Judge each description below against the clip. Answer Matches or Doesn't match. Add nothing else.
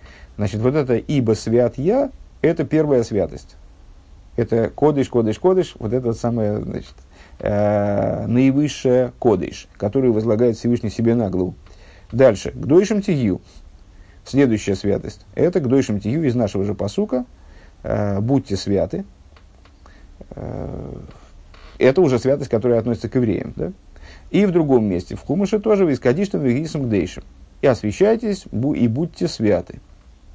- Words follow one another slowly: Doesn't match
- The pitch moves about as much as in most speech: Doesn't match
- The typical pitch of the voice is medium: Doesn't match